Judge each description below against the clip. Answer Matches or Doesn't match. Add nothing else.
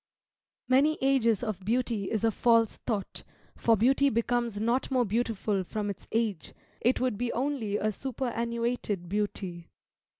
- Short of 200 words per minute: Matches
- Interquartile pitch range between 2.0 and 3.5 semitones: Matches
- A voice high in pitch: Matches